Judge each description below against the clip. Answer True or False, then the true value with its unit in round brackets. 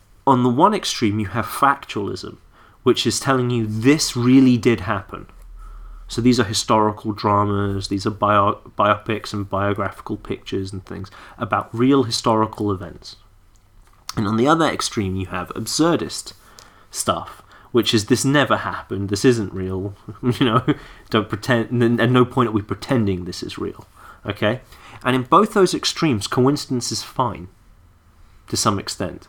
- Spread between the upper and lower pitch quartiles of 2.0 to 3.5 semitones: False (4.0 semitones)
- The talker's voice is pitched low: True (110 Hz)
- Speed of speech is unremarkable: True (155 wpm)